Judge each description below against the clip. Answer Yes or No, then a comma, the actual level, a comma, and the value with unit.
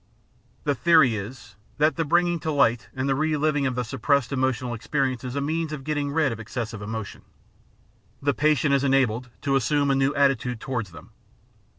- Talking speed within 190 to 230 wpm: Yes, average, 195 wpm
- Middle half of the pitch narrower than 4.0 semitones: Yes, average, 3.4 semitones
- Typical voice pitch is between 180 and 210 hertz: No, low, 135 Hz